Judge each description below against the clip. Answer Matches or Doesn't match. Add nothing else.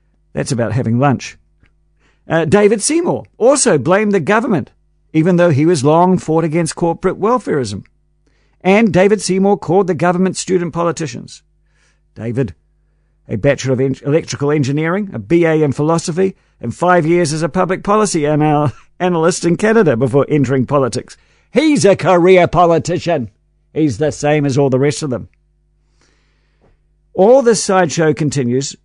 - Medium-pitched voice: Matches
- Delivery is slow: Doesn't match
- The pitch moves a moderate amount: Matches